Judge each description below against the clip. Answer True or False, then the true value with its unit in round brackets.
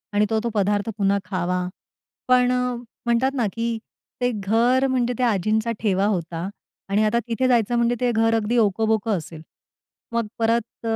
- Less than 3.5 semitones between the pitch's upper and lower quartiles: True (2.8 semitones)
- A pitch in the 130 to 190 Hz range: False (225 Hz)